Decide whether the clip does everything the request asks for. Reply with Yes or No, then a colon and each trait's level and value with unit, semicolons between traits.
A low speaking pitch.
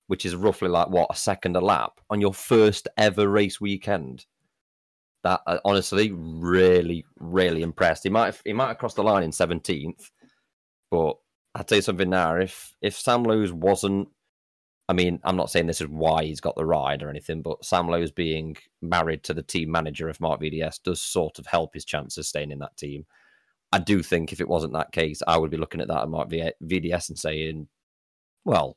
Yes: very low, 85 Hz